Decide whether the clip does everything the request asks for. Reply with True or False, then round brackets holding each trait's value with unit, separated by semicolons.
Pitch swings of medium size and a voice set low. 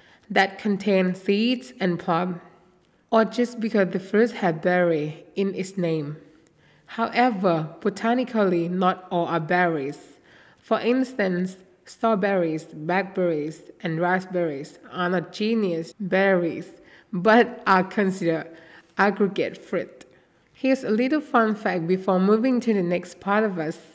False (4.0 semitones; 185 Hz)